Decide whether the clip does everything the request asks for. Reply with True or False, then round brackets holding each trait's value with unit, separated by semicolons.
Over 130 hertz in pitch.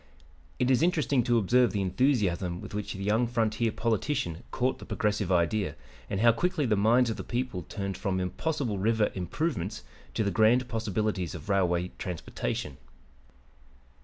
False (110 Hz)